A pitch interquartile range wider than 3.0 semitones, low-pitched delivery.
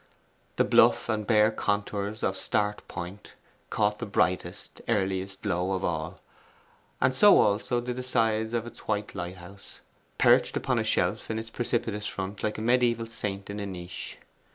No: average, 2.7 semitones; low, 105 Hz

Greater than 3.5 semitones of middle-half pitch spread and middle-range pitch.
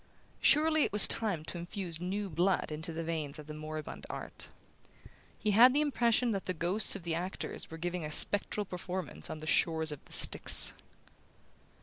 Yes: average, 4.4 semitones; medium, 175 Hz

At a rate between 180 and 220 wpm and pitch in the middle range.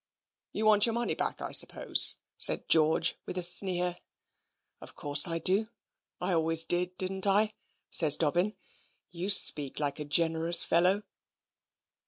No: average, 145 wpm; medium, 175 Hz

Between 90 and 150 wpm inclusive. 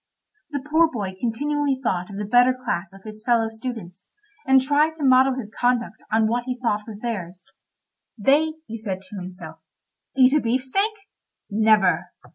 No: average, 165 wpm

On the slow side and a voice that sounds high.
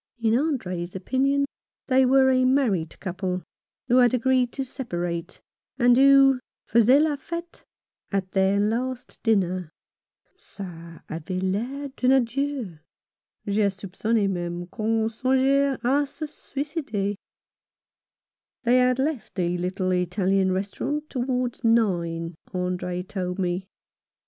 Yes: slow, 115 wpm; high, 225 Hz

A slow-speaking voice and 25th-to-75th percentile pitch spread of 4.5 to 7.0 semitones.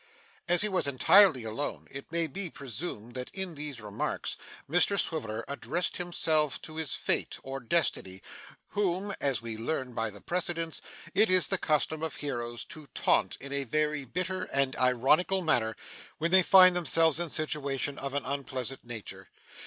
No: average, 165 wpm; average, 5.3 semitones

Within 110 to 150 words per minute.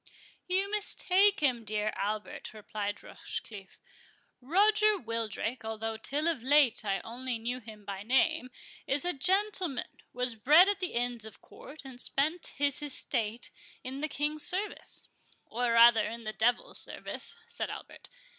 Yes: average, 145 wpm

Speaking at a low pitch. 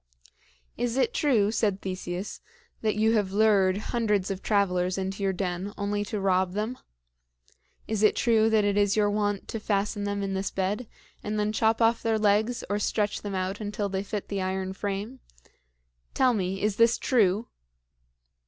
No: high, 205 Hz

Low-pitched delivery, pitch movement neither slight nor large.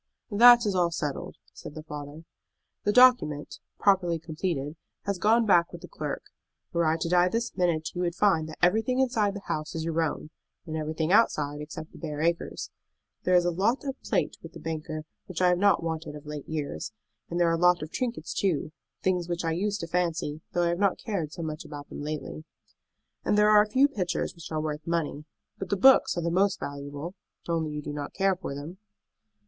No: medium, 170 Hz; average, 4.0 semitones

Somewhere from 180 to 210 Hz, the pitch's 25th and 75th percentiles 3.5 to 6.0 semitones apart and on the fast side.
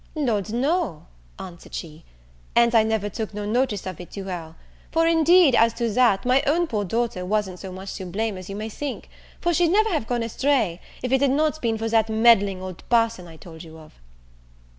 No: high, 220 Hz; wide, 5.6 semitones; fast, 210 wpm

